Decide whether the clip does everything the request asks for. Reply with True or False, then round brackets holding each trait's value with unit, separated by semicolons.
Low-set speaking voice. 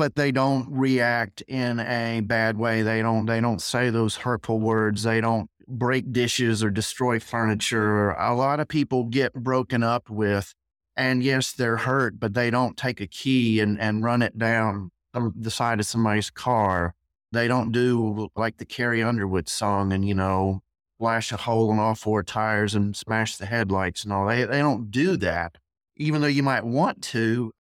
True (115 Hz)